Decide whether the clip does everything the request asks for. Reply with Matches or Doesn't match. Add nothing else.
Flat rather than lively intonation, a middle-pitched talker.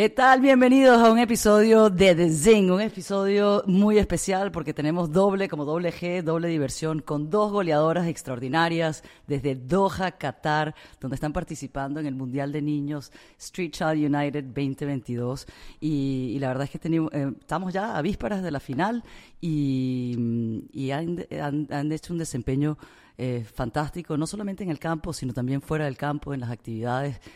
Doesn't match